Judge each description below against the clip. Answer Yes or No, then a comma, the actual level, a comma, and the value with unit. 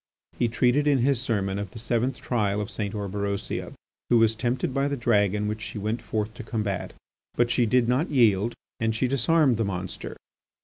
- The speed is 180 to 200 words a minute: Yes, average, 190 wpm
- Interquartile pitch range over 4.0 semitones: No, average, 3.0 semitones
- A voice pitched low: Yes, low, 115 Hz